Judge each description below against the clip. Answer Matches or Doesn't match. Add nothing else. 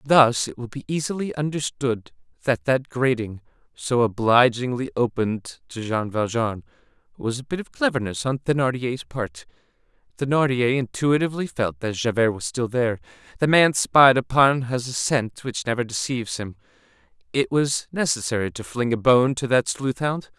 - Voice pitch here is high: Doesn't match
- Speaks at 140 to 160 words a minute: Matches